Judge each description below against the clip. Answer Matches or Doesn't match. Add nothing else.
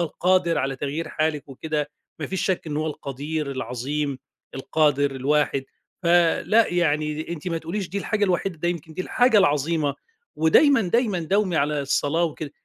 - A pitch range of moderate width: Matches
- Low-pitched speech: Doesn't match